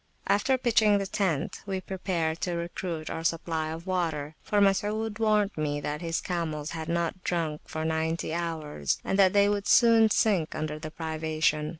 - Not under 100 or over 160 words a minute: No, average, 175 wpm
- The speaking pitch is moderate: Yes, medium, 170 Hz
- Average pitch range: Yes, average, 4.1 semitones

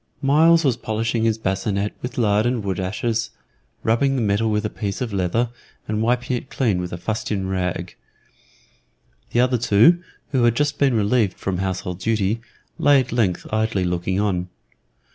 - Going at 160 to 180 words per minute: Yes, average, 170 wpm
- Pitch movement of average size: Yes, average, 4.1 semitones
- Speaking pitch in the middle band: No, low, 110 Hz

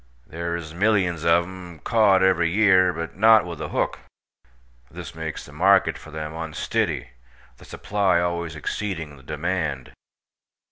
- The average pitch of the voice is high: No, very low, 85 Hz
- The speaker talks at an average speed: Yes, average, 145 wpm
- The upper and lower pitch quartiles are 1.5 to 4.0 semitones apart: Yes, average, 3.1 semitones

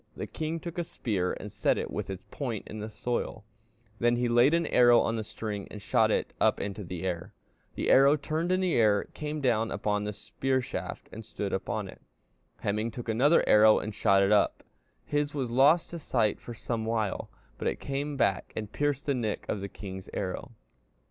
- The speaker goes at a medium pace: No, fast, 210 wpm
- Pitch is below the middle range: Yes, low, 115 Hz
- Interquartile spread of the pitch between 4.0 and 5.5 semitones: Yes, average, 5.2 semitones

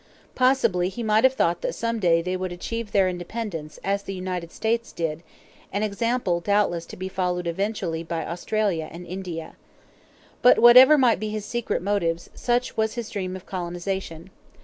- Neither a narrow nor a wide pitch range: Yes, average, 4.2 semitones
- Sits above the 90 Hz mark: Yes, high, 190 Hz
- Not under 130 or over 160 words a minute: No, average, 170 wpm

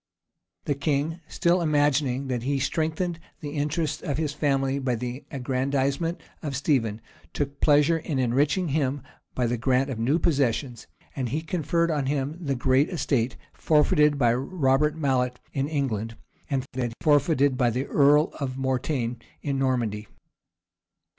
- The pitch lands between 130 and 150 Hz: Yes, medium, 140 Hz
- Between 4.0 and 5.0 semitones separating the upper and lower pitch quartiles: No, average, 2.7 semitones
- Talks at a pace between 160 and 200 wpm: No, average, 145 wpm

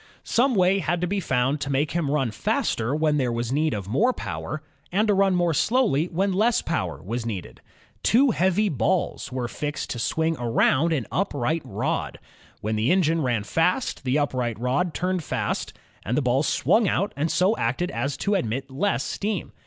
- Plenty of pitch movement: Yes, wide, 6.8 semitones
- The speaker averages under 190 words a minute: No, average, 195 wpm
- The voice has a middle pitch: Yes, medium, 155 Hz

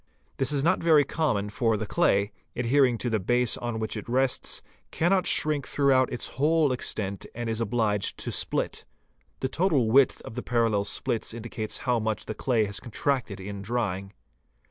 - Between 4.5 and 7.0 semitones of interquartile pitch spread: No, average, 3.9 semitones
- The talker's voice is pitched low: Yes, low, 120 Hz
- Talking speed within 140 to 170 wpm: No, average, 180 wpm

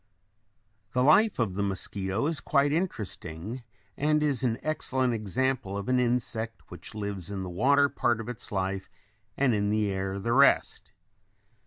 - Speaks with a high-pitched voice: No, low, 115 Hz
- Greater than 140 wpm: Yes, average, 165 wpm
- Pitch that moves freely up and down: No, average, 4.9 semitones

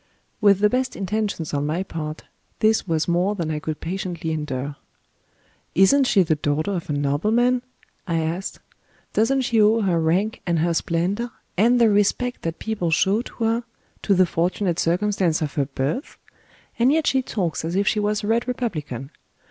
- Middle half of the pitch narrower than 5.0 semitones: No, average, 5.3 semitones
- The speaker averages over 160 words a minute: Yes, average, 180 wpm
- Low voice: No, medium, 185 Hz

